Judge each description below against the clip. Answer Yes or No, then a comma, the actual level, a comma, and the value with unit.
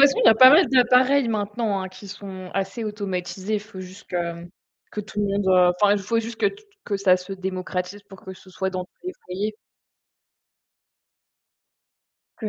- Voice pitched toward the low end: No, high, 200 Hz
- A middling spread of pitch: Yes, average, 3.0 semitones